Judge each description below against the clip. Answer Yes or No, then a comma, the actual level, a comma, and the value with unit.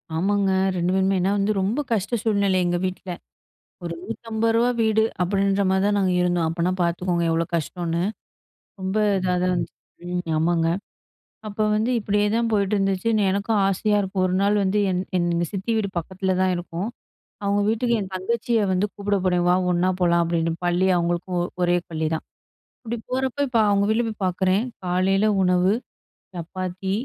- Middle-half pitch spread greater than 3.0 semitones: No, average, 2.7 semitones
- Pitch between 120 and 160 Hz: No, high, 190 Hz